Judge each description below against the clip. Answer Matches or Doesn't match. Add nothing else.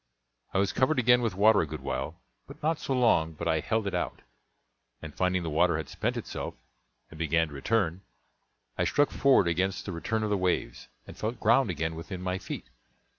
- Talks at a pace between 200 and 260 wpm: Matches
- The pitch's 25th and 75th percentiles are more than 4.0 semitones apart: Matches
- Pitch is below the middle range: Matches